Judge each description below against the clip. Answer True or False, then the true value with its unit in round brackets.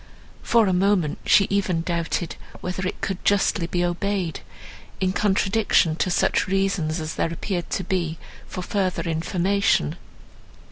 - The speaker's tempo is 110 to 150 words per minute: True (140 wpm)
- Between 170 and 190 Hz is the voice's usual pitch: True (185 Hz)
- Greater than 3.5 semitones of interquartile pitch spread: False (2.7 semitones)